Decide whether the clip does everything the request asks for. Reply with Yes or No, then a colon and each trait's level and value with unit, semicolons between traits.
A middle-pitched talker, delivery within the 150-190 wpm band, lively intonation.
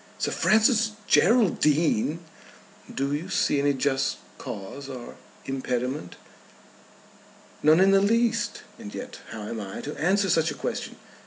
No: medium, 155 Hz; slow, 135 wpm; wide, 7.1 semitones